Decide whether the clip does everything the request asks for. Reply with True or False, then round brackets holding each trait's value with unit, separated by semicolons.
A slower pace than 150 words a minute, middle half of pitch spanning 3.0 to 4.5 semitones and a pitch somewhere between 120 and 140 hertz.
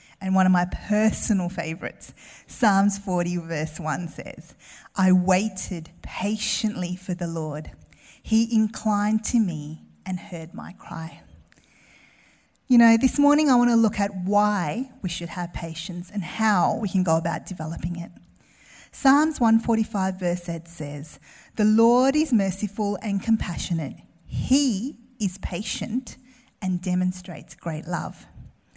False (135 wpm; 4.2 semitones; 190 Hz)